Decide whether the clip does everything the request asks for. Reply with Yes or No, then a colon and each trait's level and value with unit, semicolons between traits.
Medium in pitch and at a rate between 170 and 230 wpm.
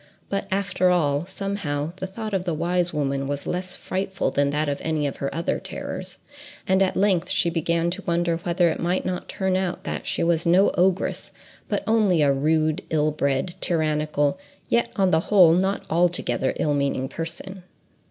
Yes: medium, 170 Hz; average, 180 wpm